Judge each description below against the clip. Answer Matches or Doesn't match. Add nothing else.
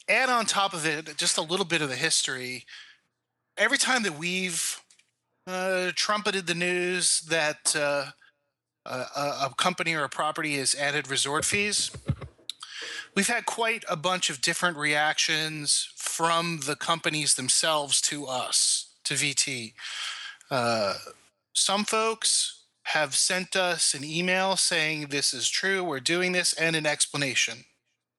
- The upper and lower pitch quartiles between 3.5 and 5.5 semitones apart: Matches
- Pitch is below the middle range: Doesn't match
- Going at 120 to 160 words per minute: Matches